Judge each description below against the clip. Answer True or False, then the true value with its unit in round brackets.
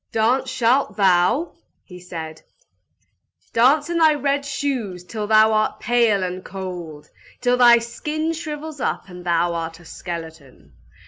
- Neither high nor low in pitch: False (220 Hz)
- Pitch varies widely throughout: True (7.6 semitones)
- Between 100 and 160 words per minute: True (140 wpm)